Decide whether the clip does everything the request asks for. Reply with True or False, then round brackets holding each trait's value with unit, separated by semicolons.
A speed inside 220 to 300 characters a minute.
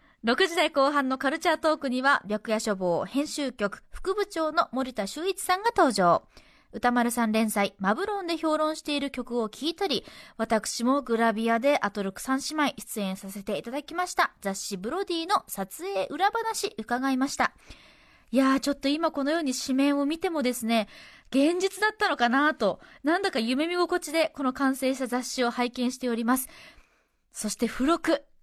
False (340 characters per minute)